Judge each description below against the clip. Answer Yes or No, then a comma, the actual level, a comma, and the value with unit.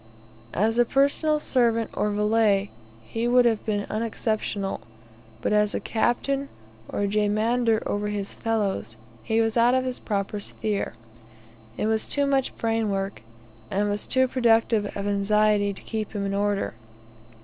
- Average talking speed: Yes, average, 150 wpm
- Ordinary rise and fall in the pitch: No, narrow, 2.3 semitones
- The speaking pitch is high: Yes, high, 215 Hz